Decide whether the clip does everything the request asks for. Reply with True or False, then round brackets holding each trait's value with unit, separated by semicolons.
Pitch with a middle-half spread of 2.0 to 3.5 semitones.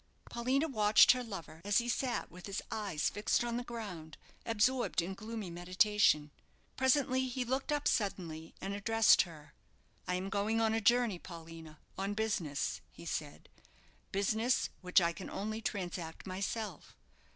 False (4.8 semitones)